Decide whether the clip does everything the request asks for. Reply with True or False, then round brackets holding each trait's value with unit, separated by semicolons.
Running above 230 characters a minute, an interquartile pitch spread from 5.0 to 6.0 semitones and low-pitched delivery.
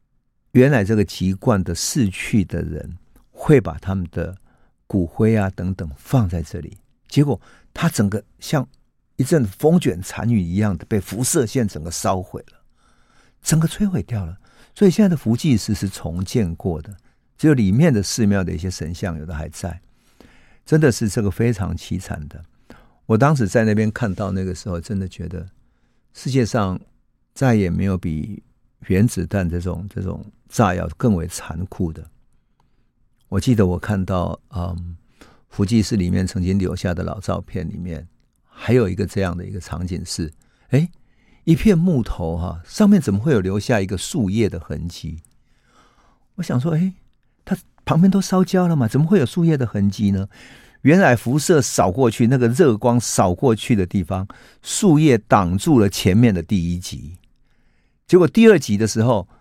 True (250 characters per minute; 5.6 semitones; 105 Hz)